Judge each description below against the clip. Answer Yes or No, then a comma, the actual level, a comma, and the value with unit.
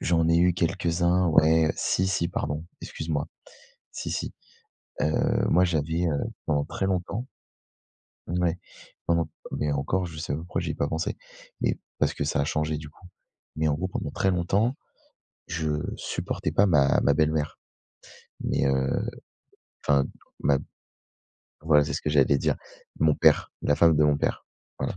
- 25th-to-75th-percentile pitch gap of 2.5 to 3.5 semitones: Yes, average, 2.8 semitones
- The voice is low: Yes, very low, 80 Hz